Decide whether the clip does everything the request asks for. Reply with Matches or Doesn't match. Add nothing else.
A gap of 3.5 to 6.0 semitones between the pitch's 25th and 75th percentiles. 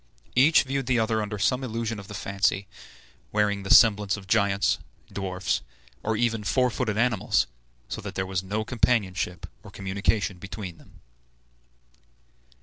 Doesn't match